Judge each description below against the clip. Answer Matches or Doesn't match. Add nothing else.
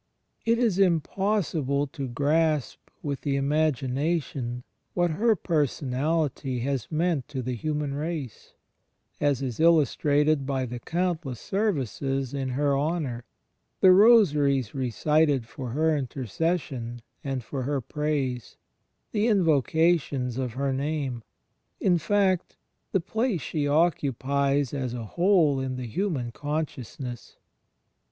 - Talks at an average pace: Doesn't match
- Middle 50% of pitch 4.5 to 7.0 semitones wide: Doesn't match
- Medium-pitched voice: Matches